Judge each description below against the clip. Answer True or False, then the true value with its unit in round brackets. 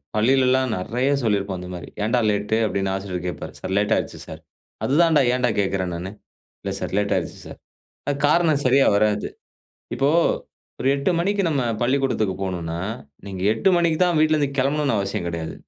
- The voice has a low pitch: True (110 Hz)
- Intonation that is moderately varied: False (6.3 semitones)